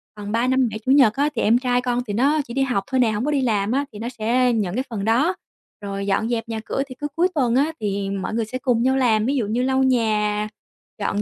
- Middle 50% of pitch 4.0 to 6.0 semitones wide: No, average, 3.6 semitones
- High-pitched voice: Yes, high, 235 Hz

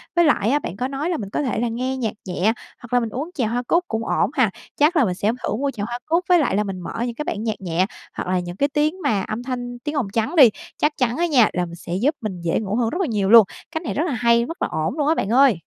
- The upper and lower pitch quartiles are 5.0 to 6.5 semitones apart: Yes, wide, 5.6 semitones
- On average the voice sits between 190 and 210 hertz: No, high, 240 Hz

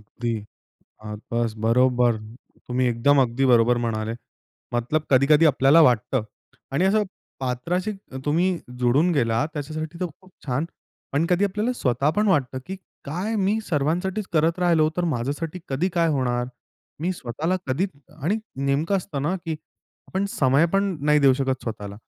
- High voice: No, medium, 145 Hz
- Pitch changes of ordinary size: No, wide, 6.1 semitones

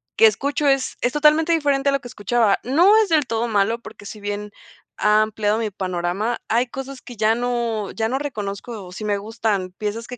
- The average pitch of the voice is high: Yes, high, 225 Hz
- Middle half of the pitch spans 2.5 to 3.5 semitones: No, average, 4.2 semitones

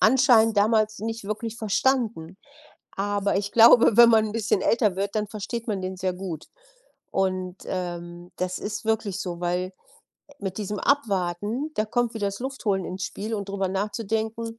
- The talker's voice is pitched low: No, high, 205 Hz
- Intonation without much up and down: No, average, 3.1 semitones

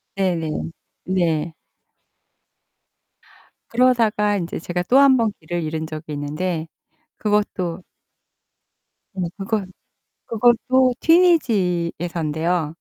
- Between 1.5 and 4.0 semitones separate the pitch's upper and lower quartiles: No, average, 5.3 semitones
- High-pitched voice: No, medium, 180 Hz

